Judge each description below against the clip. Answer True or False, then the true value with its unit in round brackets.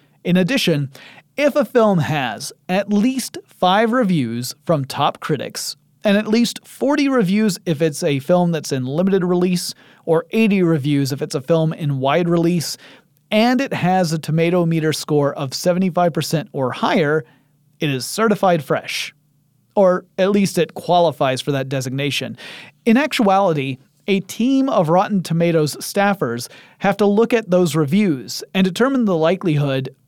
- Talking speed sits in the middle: True (155 wpm)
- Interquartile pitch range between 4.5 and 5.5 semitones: True (5.2 semitones)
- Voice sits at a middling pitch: True (170 Hz)